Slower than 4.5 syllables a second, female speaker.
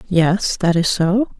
Yes: 3.4 syllables/s; female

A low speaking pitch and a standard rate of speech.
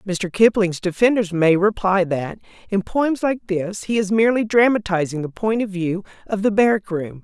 No: high, 200 Hz; average, 185 wpm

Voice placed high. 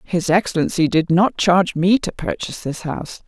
No: medium, 180 Hz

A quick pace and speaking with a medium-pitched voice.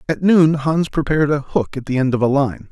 Yes: fast, 265 wpm; medium, 145 Hz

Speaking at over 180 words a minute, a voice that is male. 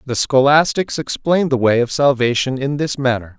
No: average, 175 wpm; male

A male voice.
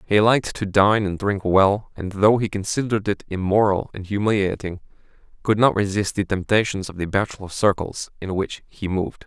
Yes: male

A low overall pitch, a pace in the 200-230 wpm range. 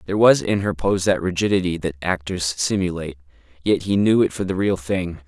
Yes: very low, 90 Hz; fast, 205 wpm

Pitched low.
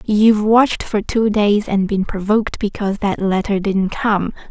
No: high, 205 Hz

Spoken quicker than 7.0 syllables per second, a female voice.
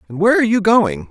No: 7.5 syllables/s; male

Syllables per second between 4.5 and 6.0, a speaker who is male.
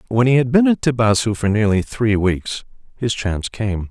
Yes: 5.0 syllables/s; male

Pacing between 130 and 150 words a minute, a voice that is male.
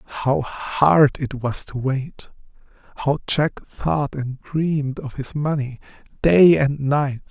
Yes: average, 140 wpm; male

